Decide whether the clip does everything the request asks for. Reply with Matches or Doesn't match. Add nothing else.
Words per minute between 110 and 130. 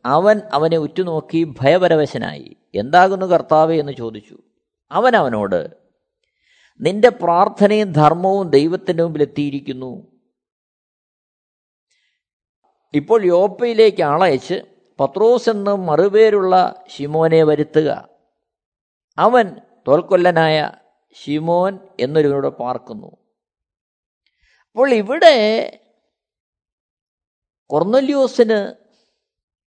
Doesn't match